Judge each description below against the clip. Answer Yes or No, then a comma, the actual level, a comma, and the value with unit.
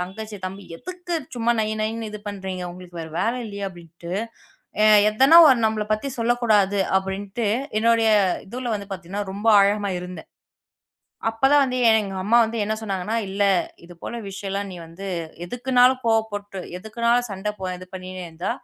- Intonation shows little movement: No, average, 3.2 semitones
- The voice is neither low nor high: No, high, 205 Hz